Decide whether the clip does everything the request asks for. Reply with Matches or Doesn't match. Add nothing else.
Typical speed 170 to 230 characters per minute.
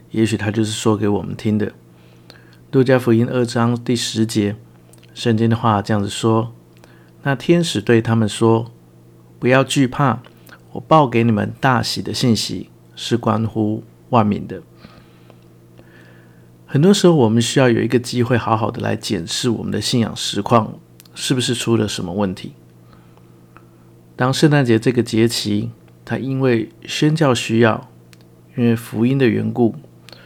Matches